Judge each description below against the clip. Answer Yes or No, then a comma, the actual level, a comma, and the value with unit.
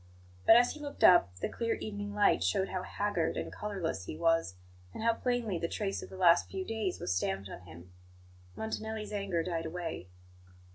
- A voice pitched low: No, high, 190 Hz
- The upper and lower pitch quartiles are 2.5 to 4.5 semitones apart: No, average, 4.9 semitones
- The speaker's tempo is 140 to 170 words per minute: No, average, 190 wpm